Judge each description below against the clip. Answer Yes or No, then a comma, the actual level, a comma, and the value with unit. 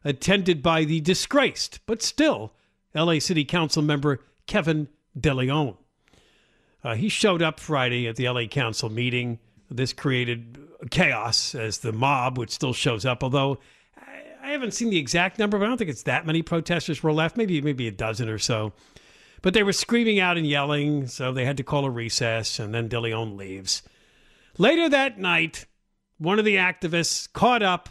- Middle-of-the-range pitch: Yes, medium, 150 Hz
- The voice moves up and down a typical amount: No, wide, 6.7 semitones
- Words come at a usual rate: Yes, average, 175 wpm